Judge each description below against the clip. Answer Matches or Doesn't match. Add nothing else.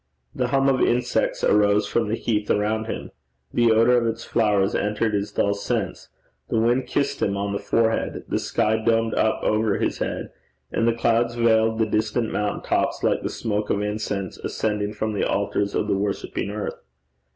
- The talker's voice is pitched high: Doesn't match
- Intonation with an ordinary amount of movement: Doesn't match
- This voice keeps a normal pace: Matches